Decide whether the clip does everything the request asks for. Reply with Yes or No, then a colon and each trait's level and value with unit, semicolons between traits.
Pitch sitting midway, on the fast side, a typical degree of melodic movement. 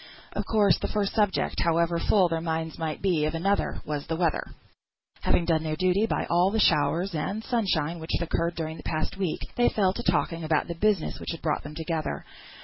Yes: medium, 170 Hz; fast, 210 wpm; average, 3.5 semitones